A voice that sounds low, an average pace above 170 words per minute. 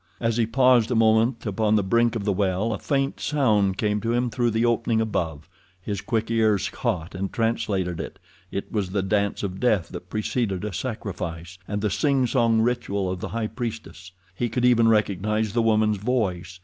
Yes: low, 110 Hz; average, 190 wpm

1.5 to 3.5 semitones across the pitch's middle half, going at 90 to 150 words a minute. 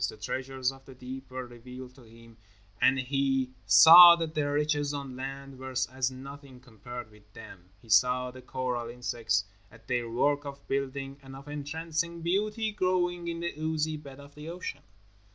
No: average, 3.0 semitones; average, 175 wpm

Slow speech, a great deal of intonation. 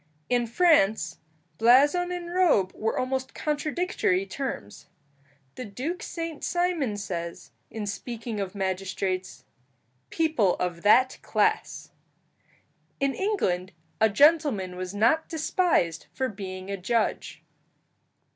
Yes: slow, 110 wpm; wide, 8.3 semitones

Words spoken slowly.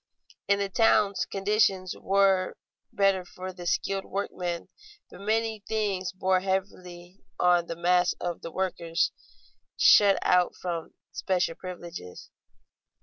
Yes: slow, 120 wpm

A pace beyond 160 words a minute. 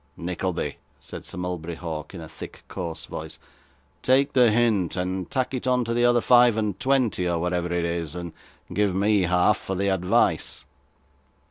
Yes: average, 170 wpm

